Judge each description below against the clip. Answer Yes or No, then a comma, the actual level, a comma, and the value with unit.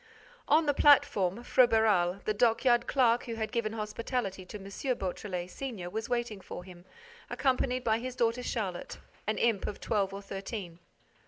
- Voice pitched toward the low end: No, high, 220 Hz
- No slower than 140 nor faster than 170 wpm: Yes, average, 160 wpm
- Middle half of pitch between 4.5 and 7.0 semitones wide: No, average, 3.9 semitones